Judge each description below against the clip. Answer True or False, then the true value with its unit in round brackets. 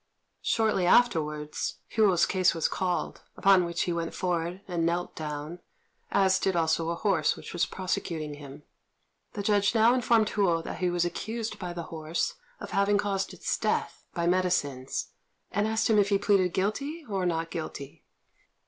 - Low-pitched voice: False (180 Hz)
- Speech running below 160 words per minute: False (165 wpm)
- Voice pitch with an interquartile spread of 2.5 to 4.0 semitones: True (3.5 semitones)